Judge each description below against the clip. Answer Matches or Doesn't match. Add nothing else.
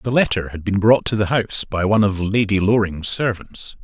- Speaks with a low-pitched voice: Matches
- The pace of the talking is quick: Matches